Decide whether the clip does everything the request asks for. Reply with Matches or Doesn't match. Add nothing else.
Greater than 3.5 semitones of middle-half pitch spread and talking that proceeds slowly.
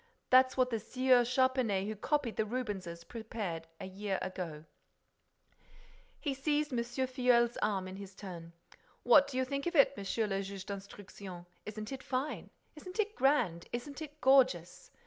Doesn't match